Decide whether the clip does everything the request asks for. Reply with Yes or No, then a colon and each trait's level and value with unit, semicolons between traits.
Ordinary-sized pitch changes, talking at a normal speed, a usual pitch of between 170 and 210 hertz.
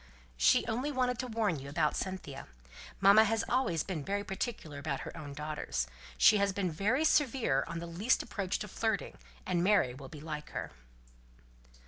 No: wide, 6.7 semitones; average, 175 wpm; high, 190 Hz